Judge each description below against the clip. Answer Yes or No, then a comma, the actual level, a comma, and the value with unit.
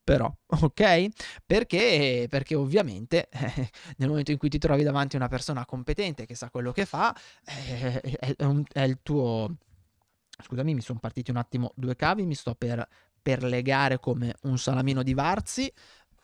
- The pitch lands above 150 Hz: No, low, 135 Hz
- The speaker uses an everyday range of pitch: Yes, average, 3.1 semitones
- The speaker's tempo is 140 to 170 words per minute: Yes, average, 165 wpm